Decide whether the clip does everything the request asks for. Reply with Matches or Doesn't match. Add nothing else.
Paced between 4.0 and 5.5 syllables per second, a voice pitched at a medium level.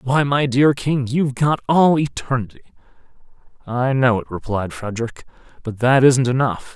Doesn't match